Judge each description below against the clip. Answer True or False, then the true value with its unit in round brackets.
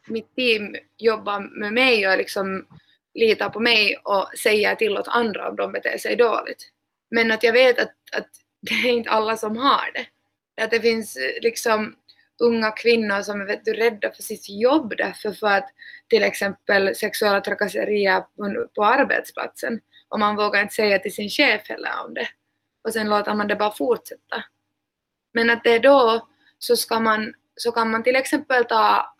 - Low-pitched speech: False (225 Hz)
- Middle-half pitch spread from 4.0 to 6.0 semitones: False (3.0 semitones)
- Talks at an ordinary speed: False (175 wpm)